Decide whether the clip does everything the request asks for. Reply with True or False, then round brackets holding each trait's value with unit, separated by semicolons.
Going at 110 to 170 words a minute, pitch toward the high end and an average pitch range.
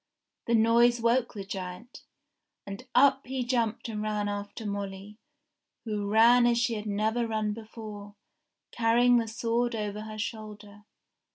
False (145 wpm; 220 Hz; 2.3 semitones)